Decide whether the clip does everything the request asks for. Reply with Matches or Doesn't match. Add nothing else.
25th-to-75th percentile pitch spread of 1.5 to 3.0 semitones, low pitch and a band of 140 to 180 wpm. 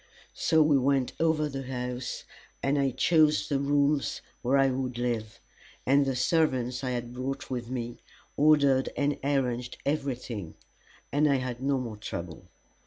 Matches